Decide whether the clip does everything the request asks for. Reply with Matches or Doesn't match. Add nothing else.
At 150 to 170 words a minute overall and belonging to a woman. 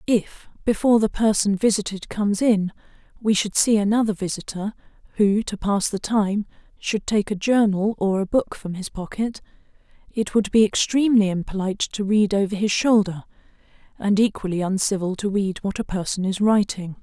Matches